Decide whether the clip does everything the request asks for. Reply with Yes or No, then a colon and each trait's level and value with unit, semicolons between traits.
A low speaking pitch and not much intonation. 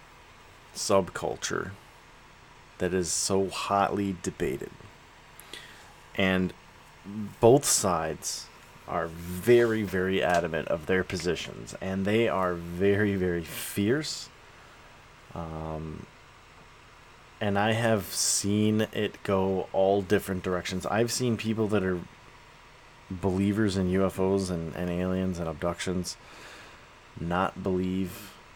Yes: very low, 95 Hz; narrow, 2.0 semitones